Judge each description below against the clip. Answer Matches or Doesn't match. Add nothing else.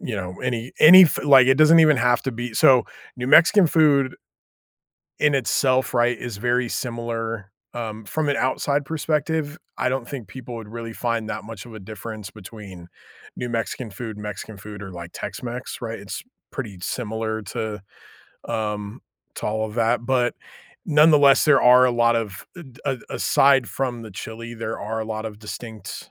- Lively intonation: Doesn't match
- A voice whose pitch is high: Doesn't match